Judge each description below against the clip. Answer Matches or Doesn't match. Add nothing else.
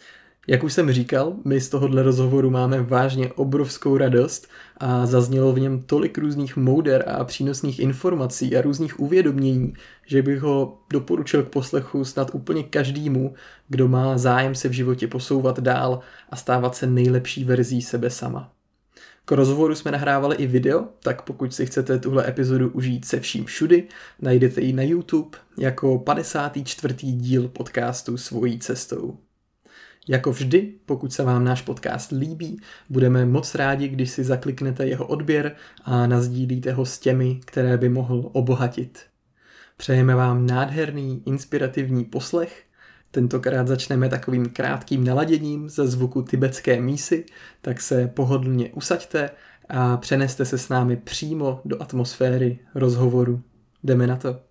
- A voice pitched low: Matches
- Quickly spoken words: Doesn't match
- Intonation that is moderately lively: Doesn't match